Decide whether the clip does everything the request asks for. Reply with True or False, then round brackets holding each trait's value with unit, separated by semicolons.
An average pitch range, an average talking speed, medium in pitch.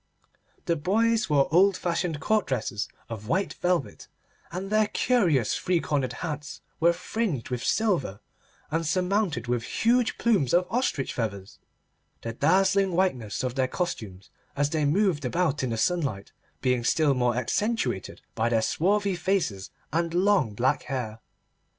False (7.5 semitones; 145 wpm; 160 Hz)